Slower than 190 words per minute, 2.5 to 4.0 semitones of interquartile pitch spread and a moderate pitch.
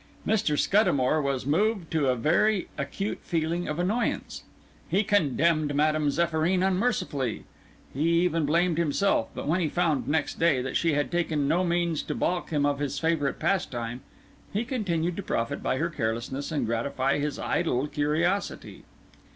Yes: average, 160 wpm; average, 3.7 semitones; medium, 160 Hz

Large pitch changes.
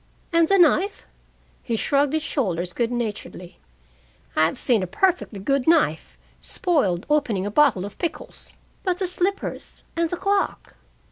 Yes: wide, 9.0 semitones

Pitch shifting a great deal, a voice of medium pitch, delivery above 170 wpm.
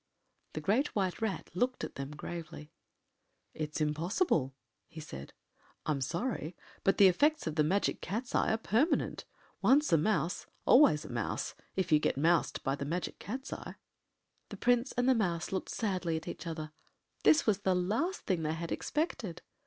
Yes: wide, 6.2 semitones; medium, 180 Hz; average, 180 wpm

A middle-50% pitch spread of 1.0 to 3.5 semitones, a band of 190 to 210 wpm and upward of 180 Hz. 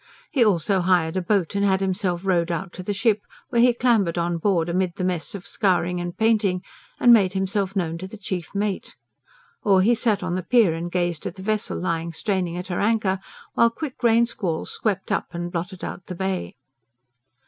Yes: average, 3.0 semitones; fast, 205 wpm; high, 190 Hz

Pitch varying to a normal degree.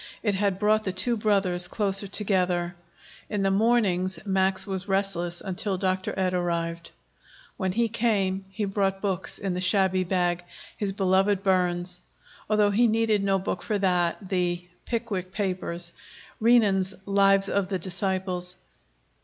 No: narrow, 1.9 semitones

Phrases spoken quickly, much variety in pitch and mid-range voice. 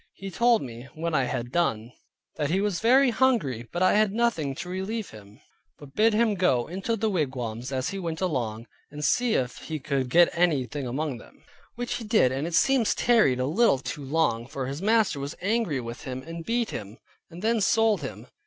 Yes: fast, 210 wpm; wide, 8.6 semitones; medium, 165 Hz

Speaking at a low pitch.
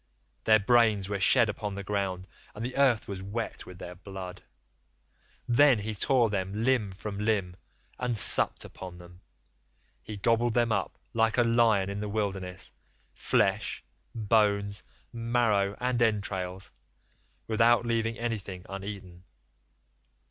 Yes: low, 105 Hz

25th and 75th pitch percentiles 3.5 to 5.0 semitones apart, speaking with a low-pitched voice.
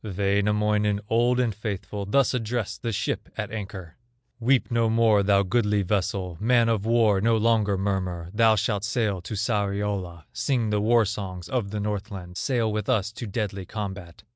No: narrow, 2.5 semitones; low, 105 Hz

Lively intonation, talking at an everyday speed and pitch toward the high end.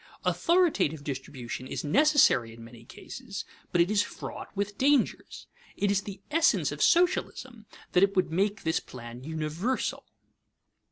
Yes: wide, 8.6 semitones; average, 145 wpm; high, 195 Hz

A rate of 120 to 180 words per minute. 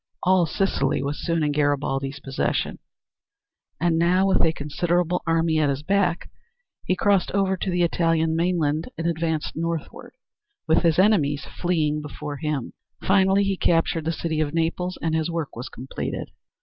Yes: average, 160 wpm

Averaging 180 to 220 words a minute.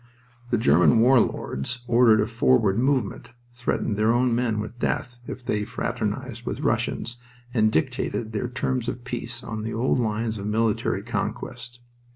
No: average, 160 wpm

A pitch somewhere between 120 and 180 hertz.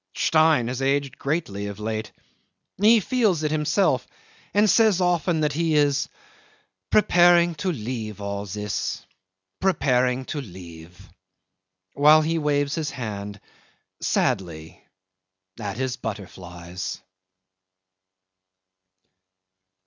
Yes: low, 135 Hz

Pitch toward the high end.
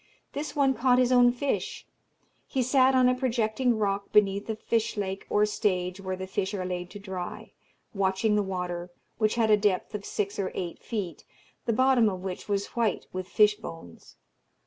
Yes: high, 210 Hz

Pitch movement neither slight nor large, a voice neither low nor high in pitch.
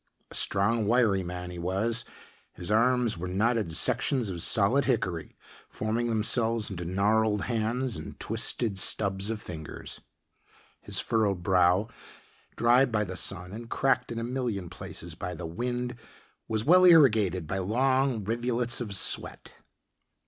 No: average, 4.4 semitones; low, 110 Hz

